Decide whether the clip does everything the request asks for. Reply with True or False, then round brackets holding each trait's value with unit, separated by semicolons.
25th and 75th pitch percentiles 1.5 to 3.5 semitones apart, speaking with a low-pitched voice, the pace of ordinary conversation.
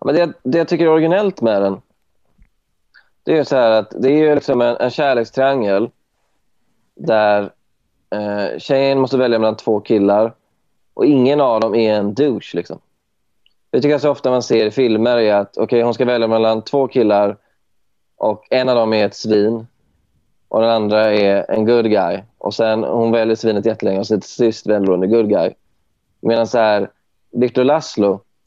True (3.2 semitones; 110 Hz; 175 wpm)